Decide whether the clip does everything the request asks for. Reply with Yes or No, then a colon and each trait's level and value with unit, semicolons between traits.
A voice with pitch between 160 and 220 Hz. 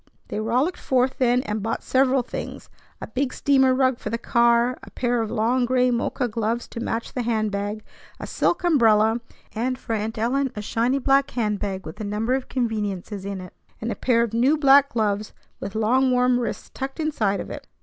No: high, 235 Hz